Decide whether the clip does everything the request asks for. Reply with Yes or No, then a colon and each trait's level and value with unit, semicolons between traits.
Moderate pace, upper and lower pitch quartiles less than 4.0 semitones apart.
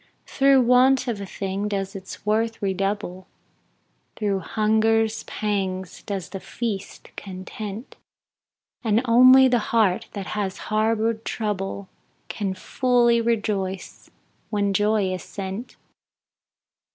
No: slow, 110 wpm; average, 2.8 semitones